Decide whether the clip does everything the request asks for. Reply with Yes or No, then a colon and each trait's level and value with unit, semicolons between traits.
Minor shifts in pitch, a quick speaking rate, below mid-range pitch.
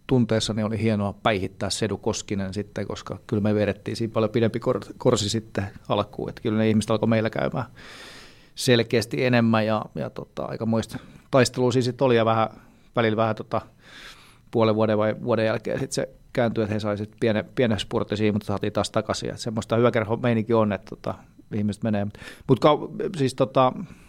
Yes: narrow, 2.2 semitones; fast, 170 wpm; low, 110 Hz